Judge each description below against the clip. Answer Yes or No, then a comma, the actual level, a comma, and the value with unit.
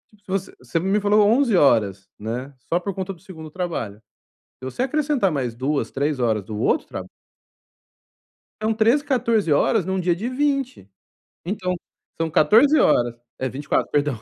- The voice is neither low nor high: Yes, medium, 180 Hz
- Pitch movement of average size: No, wide, 8.2 semitones